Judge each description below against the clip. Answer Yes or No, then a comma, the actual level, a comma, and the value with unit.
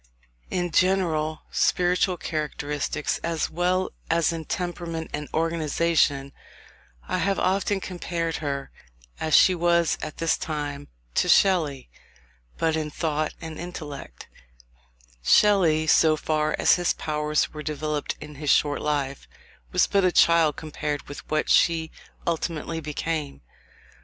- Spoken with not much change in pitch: Yes, narrow, 2.3 semitones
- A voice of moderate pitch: Yes, medium, 160 Hz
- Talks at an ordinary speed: No, slow, 125 wpm